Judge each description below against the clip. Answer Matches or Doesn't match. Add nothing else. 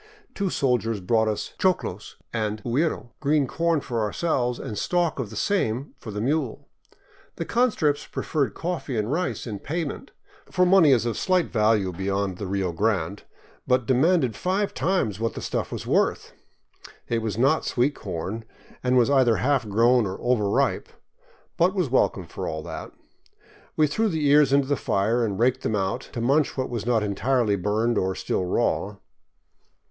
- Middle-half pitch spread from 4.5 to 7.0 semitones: Matches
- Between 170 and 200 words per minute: Matches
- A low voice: Matches